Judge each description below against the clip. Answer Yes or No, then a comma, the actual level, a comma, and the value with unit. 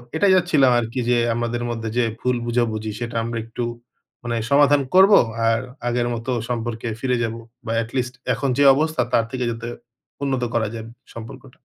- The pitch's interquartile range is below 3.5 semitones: Yes, narrow, 2.4 semitones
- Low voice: Yes, low, 120 Hz